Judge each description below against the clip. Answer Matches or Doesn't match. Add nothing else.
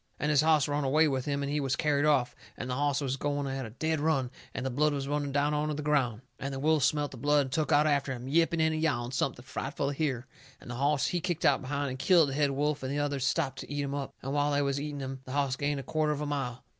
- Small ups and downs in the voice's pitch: Matches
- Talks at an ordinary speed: Doesn't match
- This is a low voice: Doesn't match